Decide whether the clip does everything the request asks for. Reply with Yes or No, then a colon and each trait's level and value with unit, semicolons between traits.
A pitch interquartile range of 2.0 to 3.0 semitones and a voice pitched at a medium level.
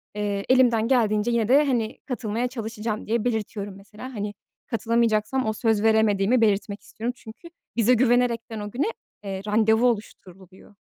No: narrow, 2.5 semitones; high, 220 Hz